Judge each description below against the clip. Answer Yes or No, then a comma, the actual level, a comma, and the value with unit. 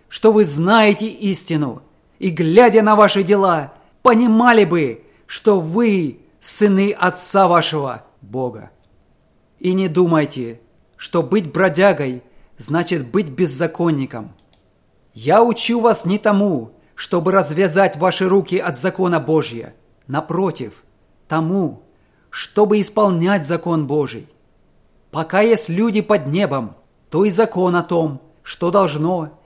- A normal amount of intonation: Yes, average, 4.8 semitones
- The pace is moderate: No, slow, 115 wpm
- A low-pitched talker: No, medium, 180 Hz